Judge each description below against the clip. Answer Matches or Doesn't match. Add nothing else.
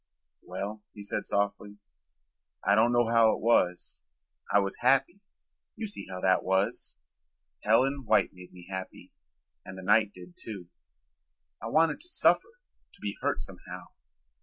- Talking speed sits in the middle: Matches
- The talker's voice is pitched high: Doesn't match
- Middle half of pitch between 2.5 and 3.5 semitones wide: Doesn't match